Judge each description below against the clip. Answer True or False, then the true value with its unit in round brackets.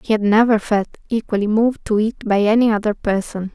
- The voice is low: False (215 Hz)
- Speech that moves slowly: False (205 wpm)